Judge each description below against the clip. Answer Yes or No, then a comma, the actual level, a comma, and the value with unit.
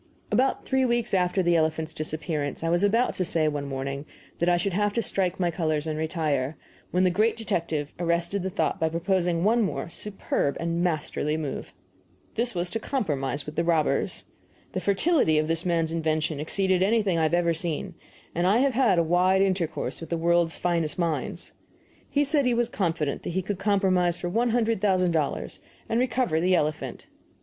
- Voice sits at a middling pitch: Yes, medium, 175 Hz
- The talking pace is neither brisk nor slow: Yes, average, 190 wpm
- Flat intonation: No, average, 3.8 semitones